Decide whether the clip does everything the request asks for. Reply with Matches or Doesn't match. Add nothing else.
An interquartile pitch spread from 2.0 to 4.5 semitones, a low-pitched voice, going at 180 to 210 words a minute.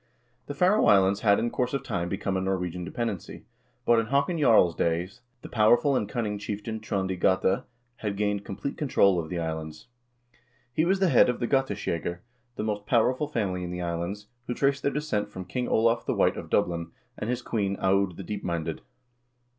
Doesn't match